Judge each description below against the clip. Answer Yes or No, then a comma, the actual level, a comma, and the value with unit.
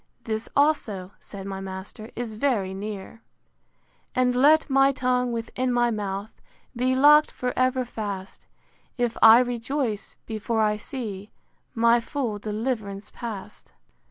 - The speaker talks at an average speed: No, slow, 130 wpm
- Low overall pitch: No, high, 230 Hz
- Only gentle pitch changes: No, average, 3.4 semitones